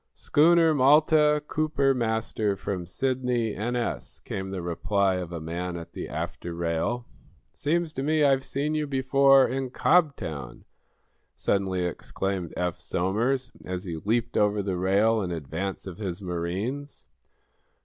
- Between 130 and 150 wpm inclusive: Yes, average, 140 wpm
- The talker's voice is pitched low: Yes, low, 105 Hz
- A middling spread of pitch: No, wide, 7.1 semitones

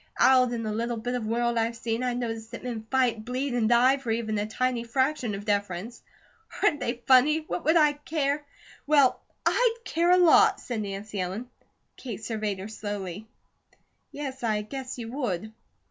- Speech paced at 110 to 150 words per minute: No, average, 185 wpm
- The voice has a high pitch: Yes, high, 235 Hz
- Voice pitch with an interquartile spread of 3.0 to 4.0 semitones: Yes, average, 3.4 semitones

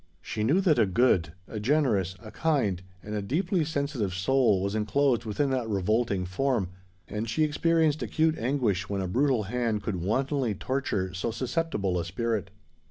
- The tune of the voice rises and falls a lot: Yes, wide, 6.3 semitones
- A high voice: No, low, 110 Hz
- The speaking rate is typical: Yes, average, 155 wpm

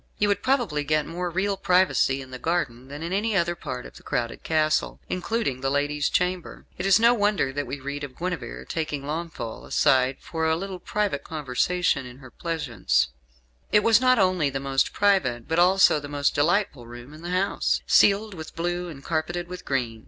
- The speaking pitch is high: No, medium, 160 Hz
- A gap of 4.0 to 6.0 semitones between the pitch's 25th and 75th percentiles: Yes, average, 5.1 semitones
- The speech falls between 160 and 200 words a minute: Yes, average, 195 wpm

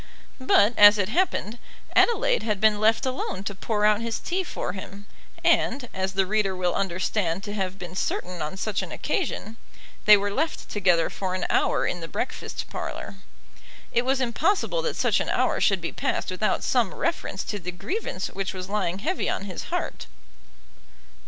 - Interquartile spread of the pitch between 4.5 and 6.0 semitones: No, average, 3.8 semitones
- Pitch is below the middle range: No, high, 205 Hz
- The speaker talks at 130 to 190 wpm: Yes, average, 180 wpm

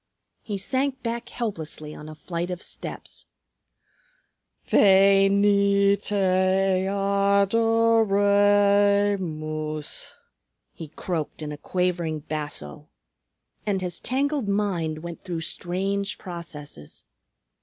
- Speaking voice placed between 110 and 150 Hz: No, high, 195 Hz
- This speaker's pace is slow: Yes, slow, 100 wpm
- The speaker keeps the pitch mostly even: No, average, 3.6 semitones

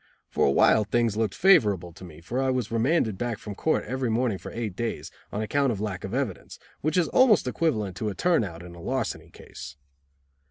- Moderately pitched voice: No, low, 110 Hz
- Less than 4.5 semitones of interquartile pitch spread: No, average, 5.2 semitones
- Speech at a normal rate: No, fast, 215 wpm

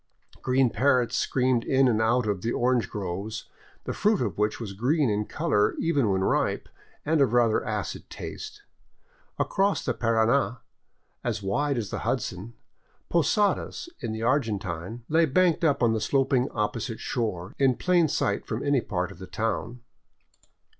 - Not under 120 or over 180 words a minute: Yes, average, 160 wpm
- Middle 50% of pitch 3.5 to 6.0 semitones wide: Yes, average, 4.9 semitones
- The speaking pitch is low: Yes, low, 120 Hz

